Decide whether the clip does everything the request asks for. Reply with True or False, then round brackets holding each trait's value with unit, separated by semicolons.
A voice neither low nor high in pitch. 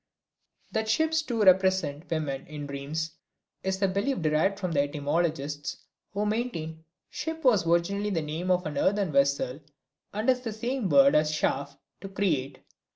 True (180 Hz)